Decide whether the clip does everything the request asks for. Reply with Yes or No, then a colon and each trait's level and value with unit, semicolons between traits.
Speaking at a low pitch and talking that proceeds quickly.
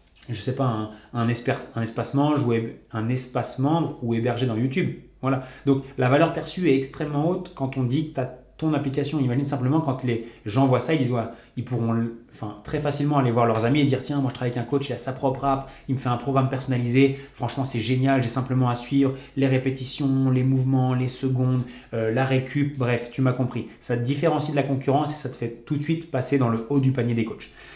Yes: low, 130 Hz; fast, 245 wpm